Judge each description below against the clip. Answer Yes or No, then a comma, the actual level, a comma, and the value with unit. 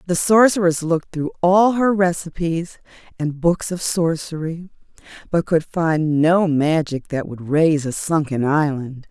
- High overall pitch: No, medium, 165 Hz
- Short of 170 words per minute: Yes, average, 145 wpm